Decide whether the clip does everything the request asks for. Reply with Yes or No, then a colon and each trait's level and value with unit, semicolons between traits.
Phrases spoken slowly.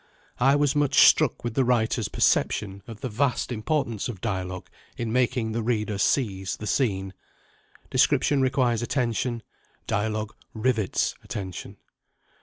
Yes: slow, 130 wpm